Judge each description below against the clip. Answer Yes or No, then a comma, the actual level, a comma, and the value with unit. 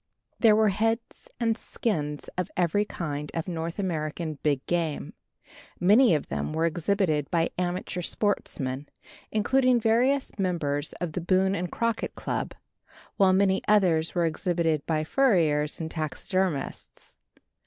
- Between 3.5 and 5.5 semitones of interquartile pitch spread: Yes, average, 4.7 semitones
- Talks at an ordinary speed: No, slow, 130 wpm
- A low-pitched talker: No, medium, 175 Hz